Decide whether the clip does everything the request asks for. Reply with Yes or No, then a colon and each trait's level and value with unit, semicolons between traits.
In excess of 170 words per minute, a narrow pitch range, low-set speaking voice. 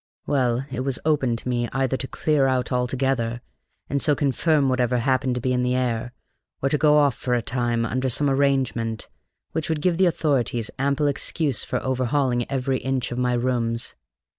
Yes: average, 190 wpm; narrow, 2.3 semitones; low, 130 Hz